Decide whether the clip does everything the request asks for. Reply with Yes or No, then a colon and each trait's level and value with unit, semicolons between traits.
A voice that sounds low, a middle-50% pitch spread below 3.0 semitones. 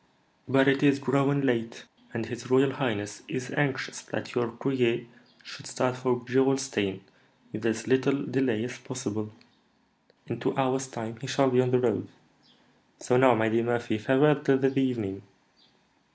Yes: low, 125 Hz; narrow, 2.6 semitones